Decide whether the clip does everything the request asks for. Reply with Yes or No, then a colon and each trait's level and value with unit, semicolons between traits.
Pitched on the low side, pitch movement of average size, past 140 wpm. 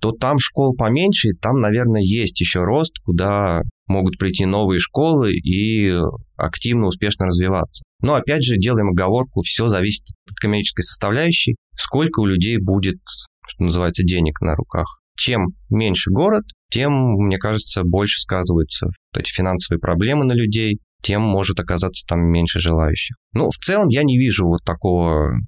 Yes: low, 100 Hz; average, 4.5 semitones; average, 155 wpm